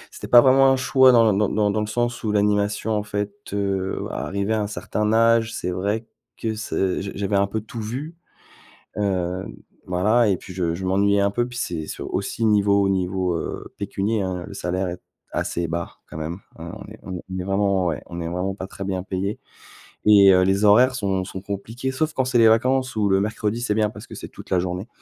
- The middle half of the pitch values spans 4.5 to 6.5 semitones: No, average, 3.0 semitones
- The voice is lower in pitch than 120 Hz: Yes, low, 100 Hz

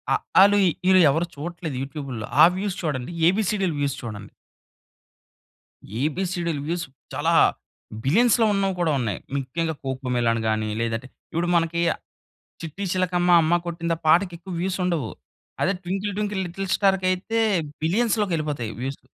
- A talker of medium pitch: Yes, medium, 170 Hz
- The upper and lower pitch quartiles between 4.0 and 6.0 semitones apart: Yes, average, 5.2 semitones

